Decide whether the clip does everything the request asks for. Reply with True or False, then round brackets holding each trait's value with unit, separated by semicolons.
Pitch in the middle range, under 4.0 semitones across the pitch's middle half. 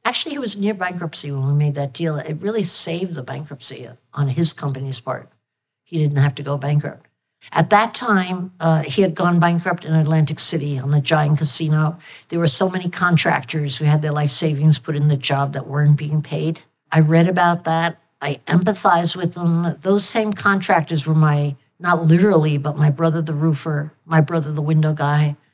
True (160 Hz; 2.7 semitones)